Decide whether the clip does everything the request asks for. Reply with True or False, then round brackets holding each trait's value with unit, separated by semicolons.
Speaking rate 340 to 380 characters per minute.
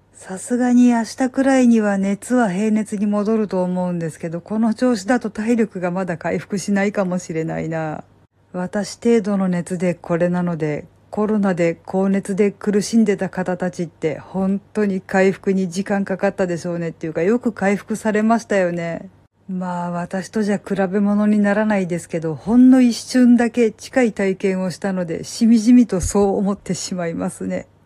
True (345 characters per minute)